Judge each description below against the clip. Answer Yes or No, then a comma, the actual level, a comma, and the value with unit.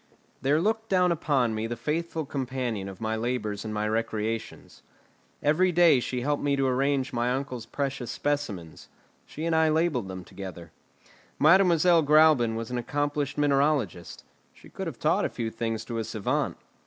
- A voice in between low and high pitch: No, low, 130 Hz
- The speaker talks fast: No, average, 165 wpm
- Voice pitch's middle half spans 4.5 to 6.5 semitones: Yes, average, 5.1 semitones